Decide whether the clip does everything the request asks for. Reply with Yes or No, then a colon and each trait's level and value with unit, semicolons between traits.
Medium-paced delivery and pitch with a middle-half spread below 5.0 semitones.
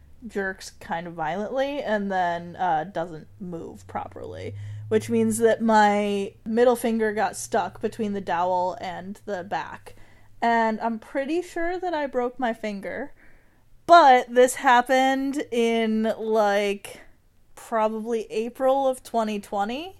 No: slow, 125 wpm; average, 3.7 semitones